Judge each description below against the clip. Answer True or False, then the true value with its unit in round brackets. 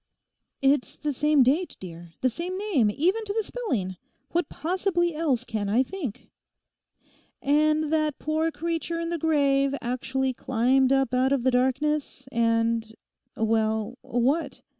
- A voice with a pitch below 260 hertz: False (275 Hz)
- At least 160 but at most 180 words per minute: False (140 wpm)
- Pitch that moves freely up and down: False (4.9 semitones)